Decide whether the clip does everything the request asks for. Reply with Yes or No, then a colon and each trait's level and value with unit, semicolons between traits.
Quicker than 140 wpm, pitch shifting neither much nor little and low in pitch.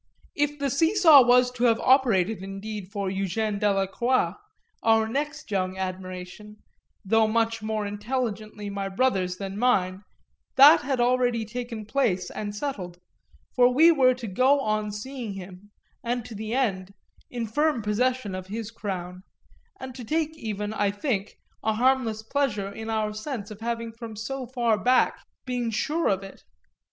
No: average, 160 wpm; average, 3.9 semitones; high, 220 Hz